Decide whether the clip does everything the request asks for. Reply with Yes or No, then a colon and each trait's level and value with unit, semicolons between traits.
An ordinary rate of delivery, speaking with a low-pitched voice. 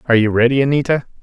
Yes: average, 195 wpm; low, 125 Hz